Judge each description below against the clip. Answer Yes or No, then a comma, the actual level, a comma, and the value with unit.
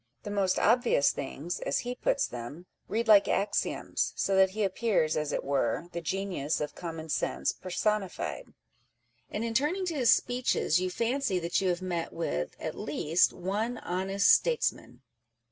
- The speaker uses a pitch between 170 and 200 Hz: Yes, high, 190 Hz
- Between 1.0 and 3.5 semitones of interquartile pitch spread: No, average, 5.2 semitones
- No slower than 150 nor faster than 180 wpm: Yes, average, 165 wpm